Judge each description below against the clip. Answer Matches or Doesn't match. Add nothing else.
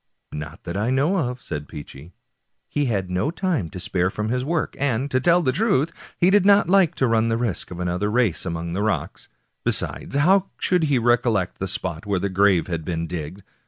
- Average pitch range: Doesn't match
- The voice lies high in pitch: Doesn't match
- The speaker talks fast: Matches